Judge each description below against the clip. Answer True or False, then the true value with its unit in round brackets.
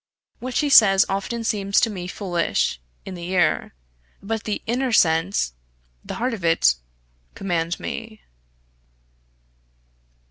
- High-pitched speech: True (195 Hz)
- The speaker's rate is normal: False (120 wpm)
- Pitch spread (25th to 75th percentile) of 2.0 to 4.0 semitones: False (4.5 semitones)